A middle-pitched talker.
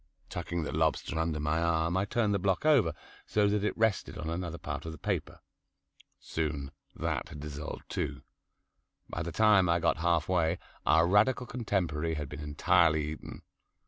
No: very low, 85 Hz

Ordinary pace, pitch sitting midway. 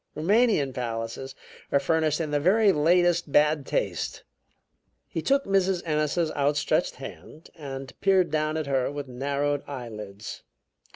No: slow, 130 wpm; medium, 150 Hz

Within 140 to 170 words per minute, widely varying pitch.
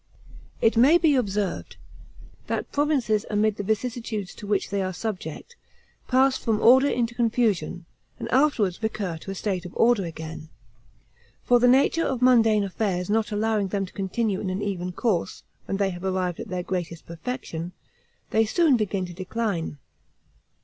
No: average, 165 wpm; average, 4.3 semitones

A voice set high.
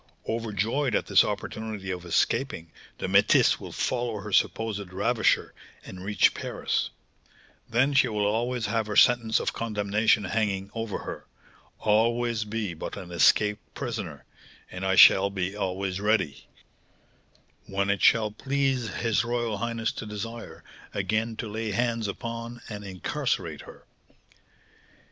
No: low, 110 Hz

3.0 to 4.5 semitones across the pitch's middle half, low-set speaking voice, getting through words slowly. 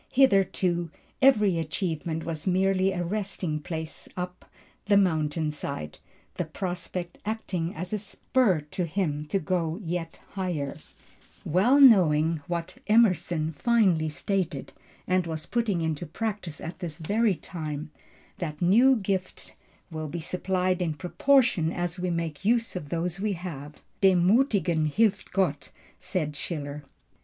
No: average, 3.5 semitones; medium, 175 Hz; slow, 130 wpm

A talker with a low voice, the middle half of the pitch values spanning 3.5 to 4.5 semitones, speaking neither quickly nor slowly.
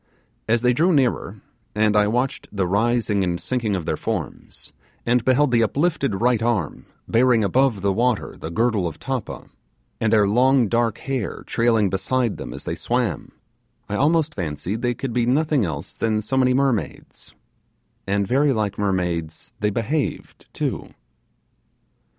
Yes: low, 115 Hz; average, 4.2 semitones; average, 155 wpm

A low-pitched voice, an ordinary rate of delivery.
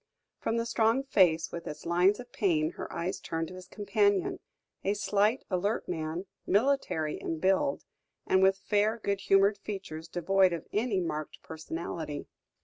No: high, 190 Hz; average, 155 wpm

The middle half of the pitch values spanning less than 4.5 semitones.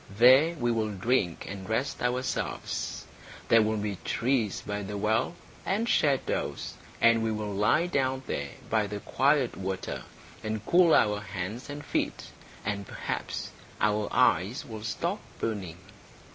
Yes: average, 4.1 semitones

